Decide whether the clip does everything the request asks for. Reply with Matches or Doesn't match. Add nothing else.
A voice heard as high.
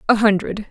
Matches